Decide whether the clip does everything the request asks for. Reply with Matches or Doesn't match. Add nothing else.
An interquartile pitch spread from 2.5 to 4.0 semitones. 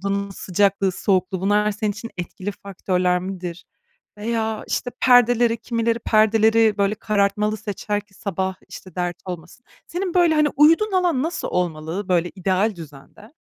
Matches